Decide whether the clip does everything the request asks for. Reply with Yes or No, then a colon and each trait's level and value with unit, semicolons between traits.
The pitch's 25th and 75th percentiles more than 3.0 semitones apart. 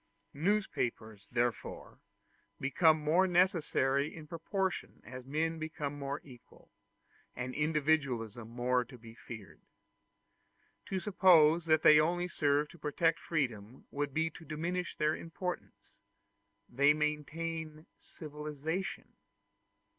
Yes: average, 3.7 semitones